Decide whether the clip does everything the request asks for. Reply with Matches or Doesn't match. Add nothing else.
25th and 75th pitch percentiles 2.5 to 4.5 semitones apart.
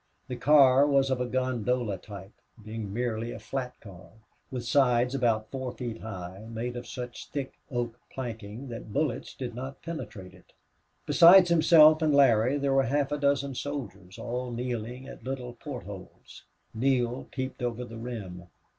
Matches